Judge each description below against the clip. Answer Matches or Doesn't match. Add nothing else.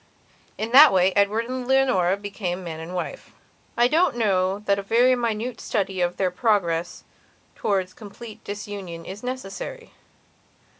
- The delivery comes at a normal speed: Matches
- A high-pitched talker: Matches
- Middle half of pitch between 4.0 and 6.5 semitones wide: Matches